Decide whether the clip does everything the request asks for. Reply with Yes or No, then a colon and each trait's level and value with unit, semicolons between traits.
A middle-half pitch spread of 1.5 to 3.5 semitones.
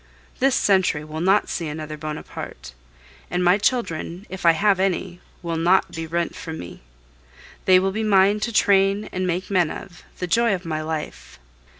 Yes: average, 3.2 semitones